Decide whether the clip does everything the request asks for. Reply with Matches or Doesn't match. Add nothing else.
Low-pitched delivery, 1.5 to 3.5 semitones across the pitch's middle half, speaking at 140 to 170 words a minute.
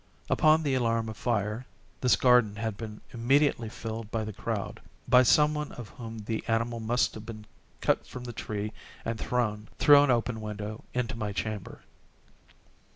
Matches